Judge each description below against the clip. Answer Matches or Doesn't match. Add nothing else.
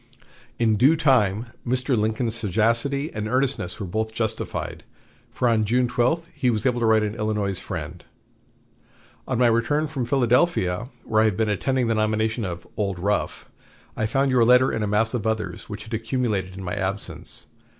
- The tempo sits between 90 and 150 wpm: Doesn't match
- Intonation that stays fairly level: Doesn't match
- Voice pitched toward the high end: Doesn't match